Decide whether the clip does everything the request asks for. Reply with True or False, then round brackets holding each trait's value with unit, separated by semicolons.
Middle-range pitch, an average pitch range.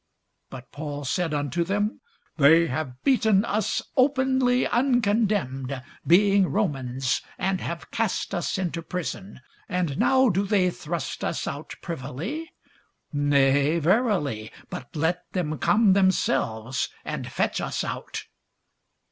False (175 Hz; 6.4 semitones)